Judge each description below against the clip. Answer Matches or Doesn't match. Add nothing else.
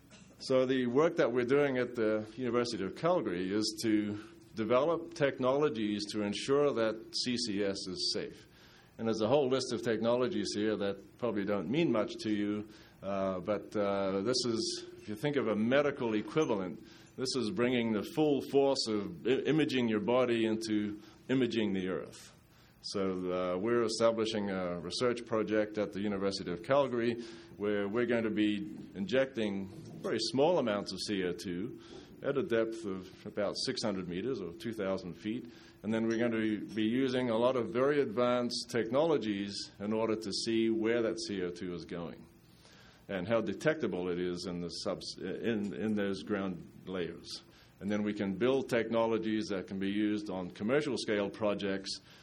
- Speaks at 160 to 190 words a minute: Matches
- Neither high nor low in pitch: Doesn't match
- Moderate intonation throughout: Matches